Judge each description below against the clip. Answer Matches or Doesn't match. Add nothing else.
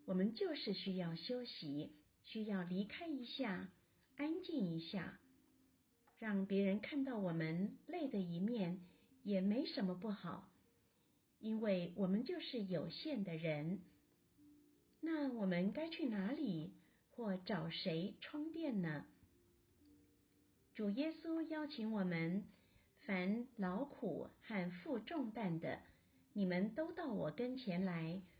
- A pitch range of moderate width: Doesn't match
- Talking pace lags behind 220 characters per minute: Matches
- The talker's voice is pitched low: Doesn't match